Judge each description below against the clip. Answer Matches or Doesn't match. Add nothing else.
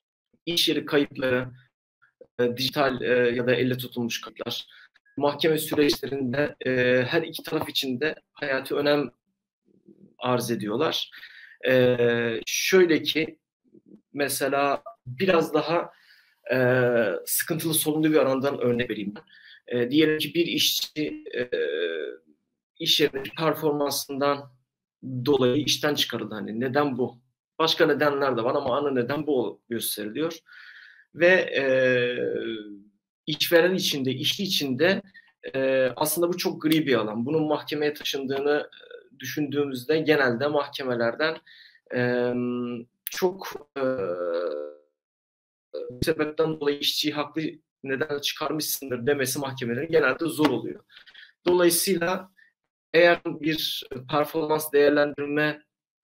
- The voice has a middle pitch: Matches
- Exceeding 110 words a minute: Doesn't match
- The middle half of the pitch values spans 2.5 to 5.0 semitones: Matches